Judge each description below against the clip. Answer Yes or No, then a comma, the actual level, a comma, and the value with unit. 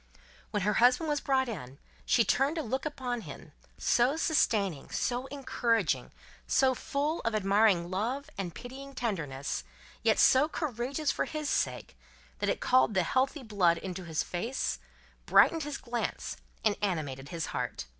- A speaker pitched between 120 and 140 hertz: No, high, 235 Hz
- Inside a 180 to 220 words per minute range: No, average, 155 wpm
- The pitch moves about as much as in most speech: No, wide, 6.3 semitones